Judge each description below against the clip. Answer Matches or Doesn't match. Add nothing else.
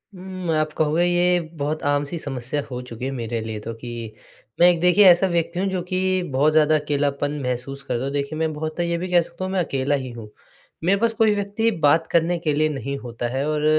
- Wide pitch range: Doesn't match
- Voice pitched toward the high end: Doesn't match